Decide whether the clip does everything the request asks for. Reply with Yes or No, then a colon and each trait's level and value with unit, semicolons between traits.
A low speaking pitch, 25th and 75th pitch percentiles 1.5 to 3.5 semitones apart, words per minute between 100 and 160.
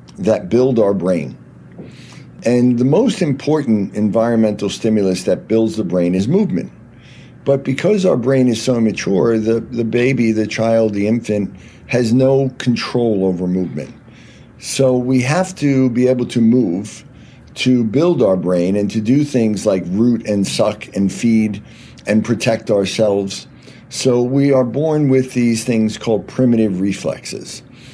Yes: low, 115 Hz; average, 3.2 semitones; average, 150 wpm